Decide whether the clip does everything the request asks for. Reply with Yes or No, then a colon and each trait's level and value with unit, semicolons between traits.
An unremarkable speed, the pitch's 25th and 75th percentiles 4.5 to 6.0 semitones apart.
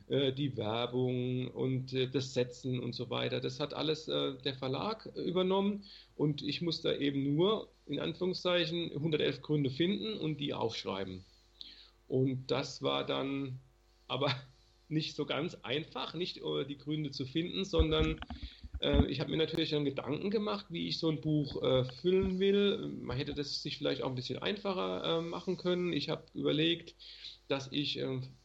Yes: average, 165 wpm; average, 4.9 semitones